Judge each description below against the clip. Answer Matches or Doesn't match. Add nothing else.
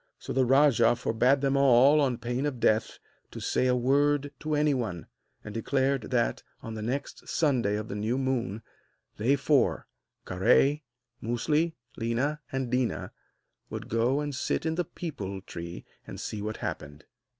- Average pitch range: Matches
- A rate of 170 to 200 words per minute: Doesn't match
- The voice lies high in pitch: Doesn't match